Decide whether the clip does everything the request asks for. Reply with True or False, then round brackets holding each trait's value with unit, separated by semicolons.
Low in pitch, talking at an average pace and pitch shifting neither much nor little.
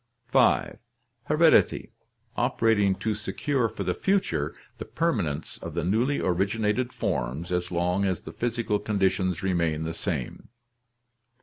False (100 Hz; 125 wpm; 4.7 semitones)